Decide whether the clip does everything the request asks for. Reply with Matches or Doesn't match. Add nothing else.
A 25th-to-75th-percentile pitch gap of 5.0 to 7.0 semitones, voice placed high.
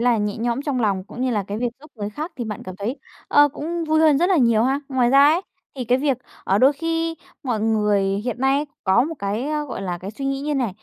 Matches